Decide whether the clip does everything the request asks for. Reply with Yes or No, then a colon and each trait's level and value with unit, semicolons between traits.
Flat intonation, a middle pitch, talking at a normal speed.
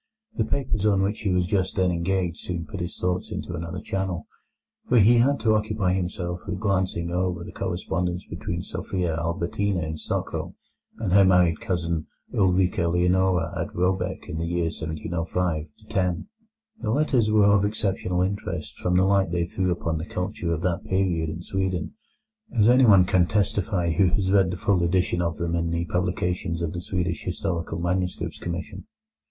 No: narrow, 2.1 semitones; very low, 90 Hz; average, 175 wpm